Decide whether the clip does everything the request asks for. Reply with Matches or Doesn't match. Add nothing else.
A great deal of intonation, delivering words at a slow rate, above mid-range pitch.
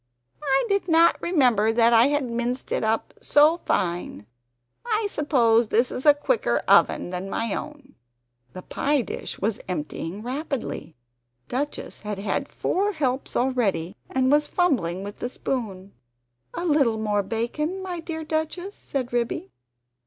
Doesn't match